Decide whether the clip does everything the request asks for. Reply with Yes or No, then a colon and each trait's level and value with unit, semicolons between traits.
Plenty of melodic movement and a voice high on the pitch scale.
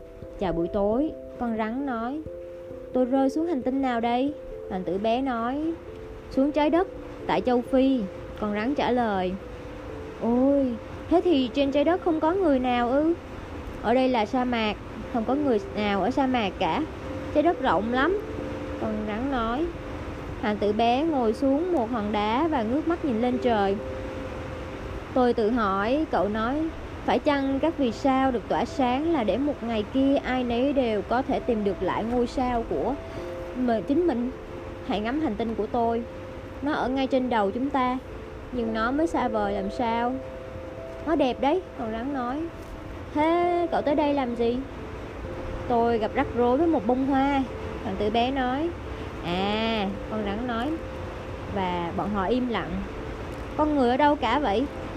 No: average, 3.8 semitones; very high, 250 Hz